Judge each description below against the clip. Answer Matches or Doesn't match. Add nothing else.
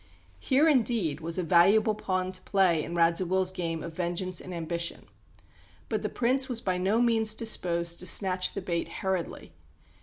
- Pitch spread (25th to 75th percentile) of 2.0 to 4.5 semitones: Matches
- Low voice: Doesn't match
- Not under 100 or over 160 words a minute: Doesn't match